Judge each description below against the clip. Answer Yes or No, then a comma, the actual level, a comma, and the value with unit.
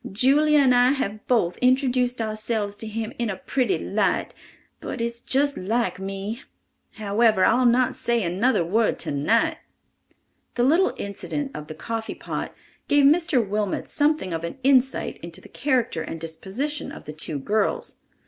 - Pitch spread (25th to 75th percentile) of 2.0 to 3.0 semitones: No, average, 4.7 semitones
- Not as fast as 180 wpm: Yes, average, 155 wpm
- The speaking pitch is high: Yes, high, 230 Hz